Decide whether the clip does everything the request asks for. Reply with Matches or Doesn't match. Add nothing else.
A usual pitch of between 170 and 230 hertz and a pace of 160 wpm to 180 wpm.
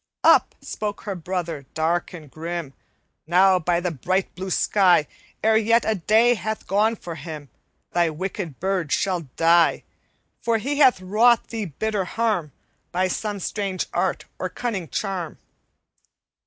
Doesn't match